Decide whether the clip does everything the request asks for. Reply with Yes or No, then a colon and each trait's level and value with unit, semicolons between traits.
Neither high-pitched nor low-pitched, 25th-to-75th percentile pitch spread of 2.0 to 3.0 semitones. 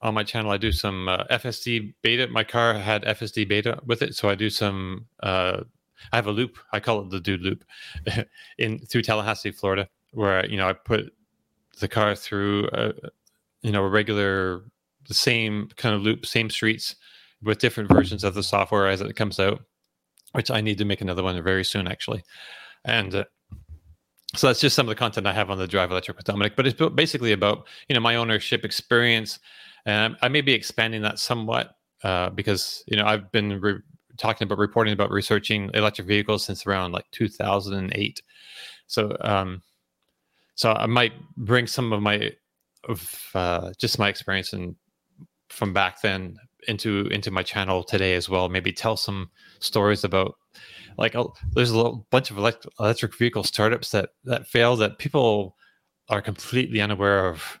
No: low, 105 Hz; average, 2.7 semitones